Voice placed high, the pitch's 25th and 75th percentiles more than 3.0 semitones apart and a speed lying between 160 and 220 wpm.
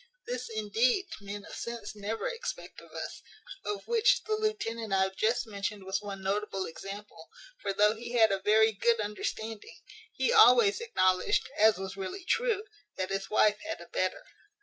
Yes: high, 215 Hz; average, 4.1 semitones; average, 170 wpm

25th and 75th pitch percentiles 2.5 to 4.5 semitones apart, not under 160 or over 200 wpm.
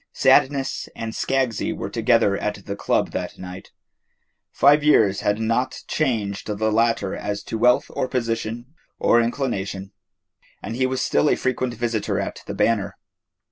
No: average, 3.8 semitones; average, 150 wpm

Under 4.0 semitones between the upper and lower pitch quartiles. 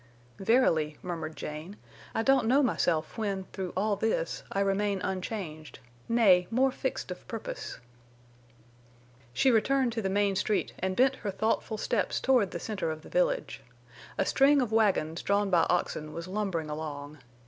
No: wide, 5.4 semitones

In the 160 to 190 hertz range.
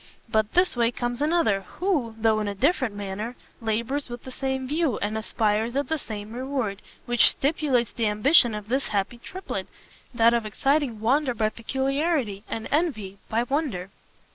No: high, 240 Hz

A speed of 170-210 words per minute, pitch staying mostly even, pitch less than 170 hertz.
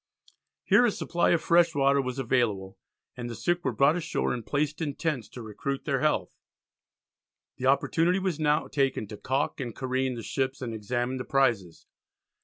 No: average, 180 wpm; average, 3.9 semitones; low, 135 Hz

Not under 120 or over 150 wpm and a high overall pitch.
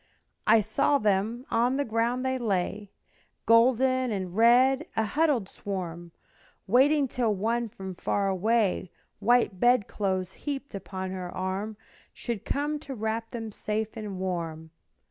Yes: average, 140 wpm; high, 220 Hz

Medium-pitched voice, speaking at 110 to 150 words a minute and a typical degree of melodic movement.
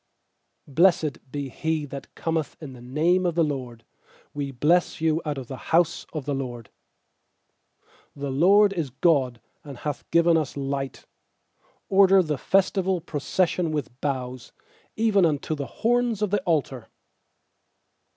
Yes: medium, 155 Hz; average, 140 wpm; average, 4.4 semitones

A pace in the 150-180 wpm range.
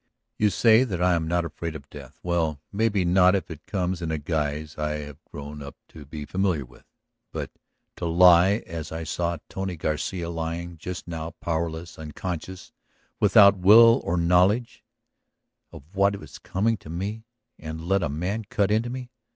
Yes: average, 175 wpm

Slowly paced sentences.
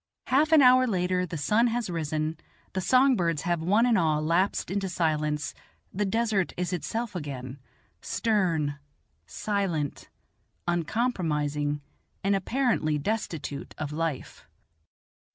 Yes: slow, 120 wpm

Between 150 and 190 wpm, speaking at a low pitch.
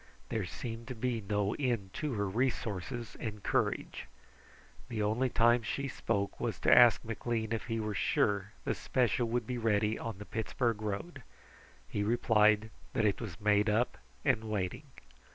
Yes: average, 165 wpm; low, 110 Hz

